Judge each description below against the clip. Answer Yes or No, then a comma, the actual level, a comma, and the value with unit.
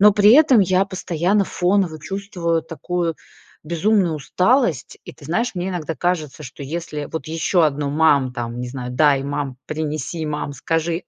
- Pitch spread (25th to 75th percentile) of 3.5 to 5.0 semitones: Yes, average, 4.0 semitones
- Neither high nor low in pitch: Yes, medium, 165 Hz